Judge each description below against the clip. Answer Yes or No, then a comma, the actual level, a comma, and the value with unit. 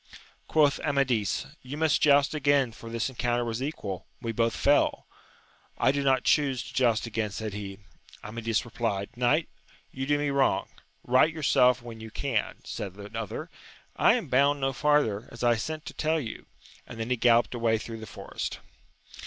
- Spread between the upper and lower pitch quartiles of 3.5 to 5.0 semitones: Yes, average, 3.9 semitones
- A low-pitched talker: Yes, low, 120 Hz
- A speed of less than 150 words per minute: No, average, 180 wpm